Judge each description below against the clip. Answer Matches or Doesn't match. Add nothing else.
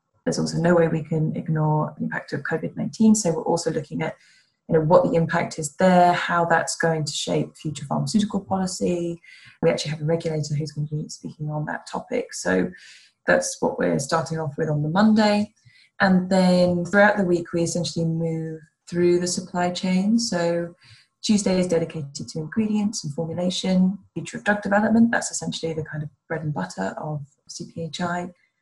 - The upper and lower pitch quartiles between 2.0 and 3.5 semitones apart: Matches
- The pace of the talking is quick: Doesn't match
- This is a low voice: Doesn't match